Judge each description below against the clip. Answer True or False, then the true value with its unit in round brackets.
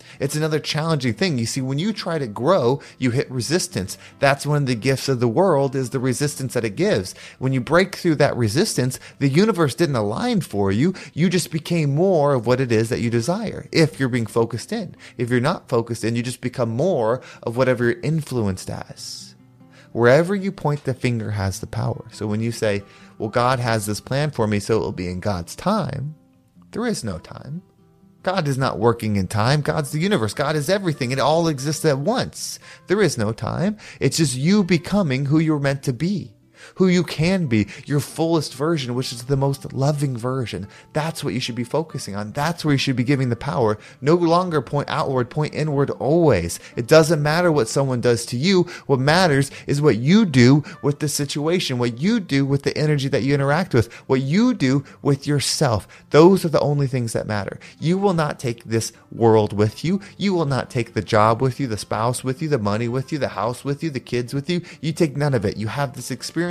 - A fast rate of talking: True (220 wpm)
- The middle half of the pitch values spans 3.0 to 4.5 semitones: False (5.1 semitones)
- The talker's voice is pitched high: False (140 Hz)